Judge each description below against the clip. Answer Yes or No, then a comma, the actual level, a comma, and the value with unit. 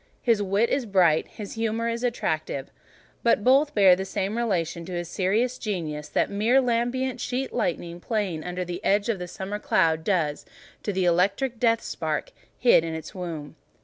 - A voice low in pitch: No, high, 195 Hz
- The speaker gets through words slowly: No, average, 180 wpm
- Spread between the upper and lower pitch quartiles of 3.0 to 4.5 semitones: No, average, 5.0 semitones